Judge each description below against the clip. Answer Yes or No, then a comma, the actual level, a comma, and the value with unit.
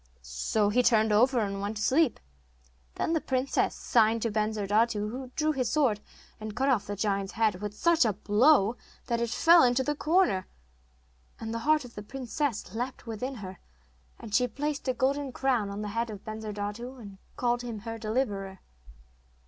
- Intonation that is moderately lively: Yes, average, 3.9 semitones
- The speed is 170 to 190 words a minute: Yes, average, 180 wpm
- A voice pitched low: No, high, 230 Hz